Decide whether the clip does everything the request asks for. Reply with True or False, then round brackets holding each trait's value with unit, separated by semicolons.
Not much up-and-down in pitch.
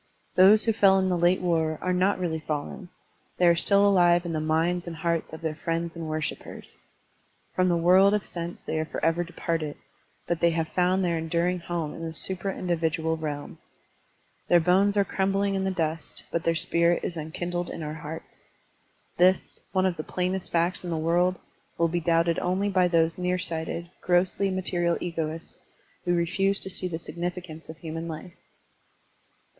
True (2.0 semitones)